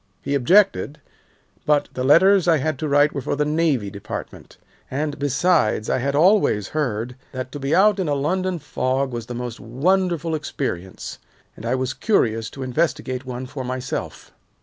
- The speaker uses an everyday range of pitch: Yes, average, 4.1 semitones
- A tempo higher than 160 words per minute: Yes, average, 170 wpm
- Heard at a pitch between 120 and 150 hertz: Yes, medium, 140 Hz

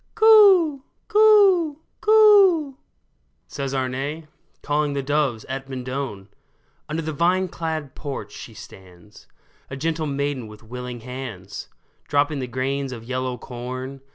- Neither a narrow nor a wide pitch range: Yes, average, 5.0 semitones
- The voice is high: No, medium, 140 Hz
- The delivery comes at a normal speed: No, slow, 125 wpm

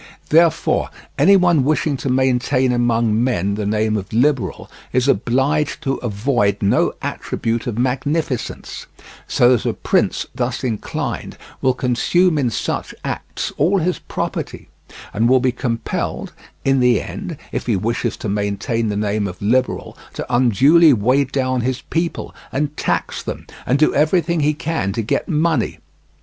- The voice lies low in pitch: Yes, low, 125 Hz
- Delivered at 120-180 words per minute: Yes, average, 155 wpm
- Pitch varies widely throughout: No, average, 4.6 semitones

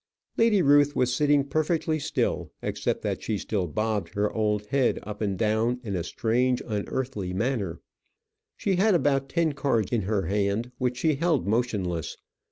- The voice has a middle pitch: No, low, 120 Hz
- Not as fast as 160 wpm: No, average, 165 wpm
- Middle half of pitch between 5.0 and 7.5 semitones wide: Yes, wide, 5.4 semitones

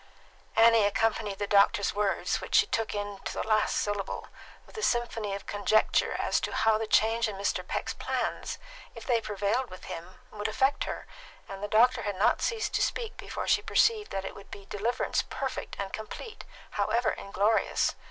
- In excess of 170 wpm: Yes, average, 185 wpm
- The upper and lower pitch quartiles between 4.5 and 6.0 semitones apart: No, narrow, 2.4 semitones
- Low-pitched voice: No, high, 215 Hz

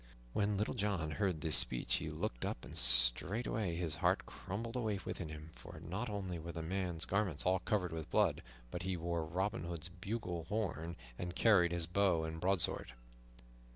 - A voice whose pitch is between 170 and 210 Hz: No, very low, 90 Hz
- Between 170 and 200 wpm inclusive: Yes, average, 180 wpm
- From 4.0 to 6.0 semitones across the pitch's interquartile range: No, average, 3.6 semitones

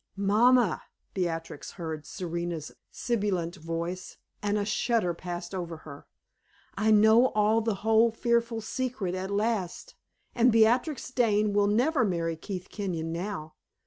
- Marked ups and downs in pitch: No, average, 4.6 semitones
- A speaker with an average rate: No, slow, 130 wpm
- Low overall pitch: No, high, 205 Hz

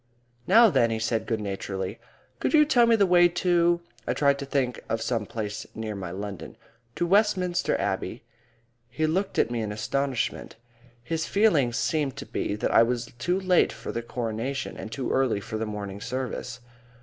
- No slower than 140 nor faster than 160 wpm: No, average, 185 wpm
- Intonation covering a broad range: Yes, wide, 7.8 semitones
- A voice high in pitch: No, low, 125 Hz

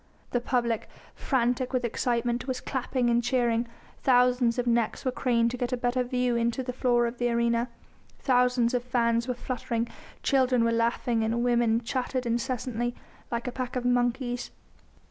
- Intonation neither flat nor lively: No, narrow, 1.2 semitones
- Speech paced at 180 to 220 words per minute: No, average, 165 wpm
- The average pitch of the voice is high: Yes, high, 245 Hz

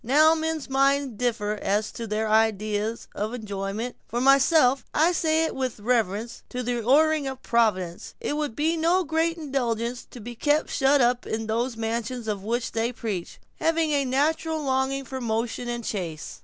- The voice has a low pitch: No, high, 245 Hz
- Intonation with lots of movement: No, average, 4.5 semitones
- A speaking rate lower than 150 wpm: No, average, 185 wpm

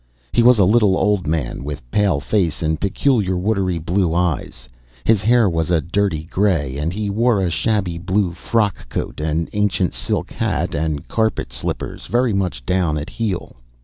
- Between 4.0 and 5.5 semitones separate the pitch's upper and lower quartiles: Yes, average, 4.5 semitones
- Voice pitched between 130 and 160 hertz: No, very low, 95 Hz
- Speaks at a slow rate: No, average, 175 wpm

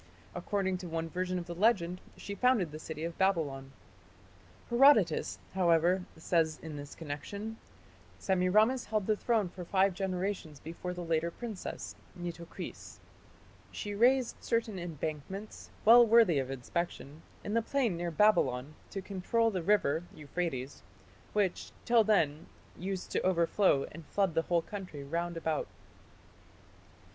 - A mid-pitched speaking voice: Yes, medium, 180 Hz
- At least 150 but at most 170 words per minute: No, slow, 135 wpm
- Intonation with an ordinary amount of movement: Yes, average, 4.0 semitones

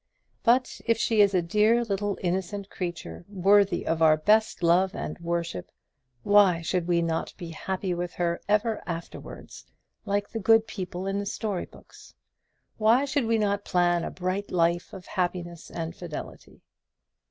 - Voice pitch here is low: No, medium, 185 Hz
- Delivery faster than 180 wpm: No, average, 160 wpm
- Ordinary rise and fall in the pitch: Yes, average, 3.1 semitones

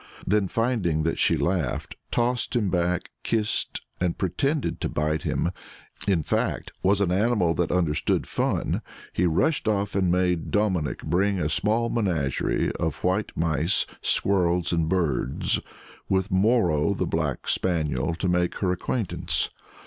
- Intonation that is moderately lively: Yes, average, 3.7 semitones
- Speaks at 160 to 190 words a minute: No, average, 140 wpm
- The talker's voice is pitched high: No, very low, 90 Hz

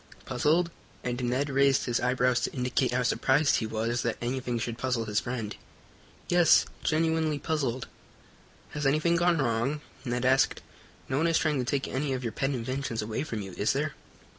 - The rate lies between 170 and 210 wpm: Yes, average, 180 wpm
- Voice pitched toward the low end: Yes, low, 130 Hz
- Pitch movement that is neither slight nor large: Yes, average, 3.6 semitones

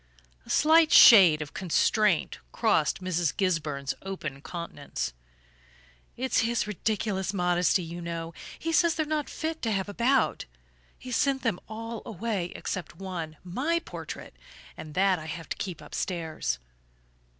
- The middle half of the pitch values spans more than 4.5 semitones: Yes, wide, 5.6 semitones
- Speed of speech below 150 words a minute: Yes, average, 140 wpm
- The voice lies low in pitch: No, high, 190 Hz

